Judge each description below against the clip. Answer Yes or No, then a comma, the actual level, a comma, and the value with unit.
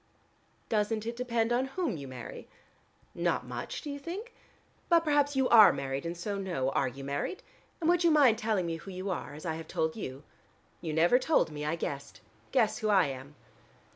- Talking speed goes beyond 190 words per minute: Yes, average, 200 wpm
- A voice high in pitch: Yes, high, 200 Hz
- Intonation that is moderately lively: No, wide, 8.9 semitones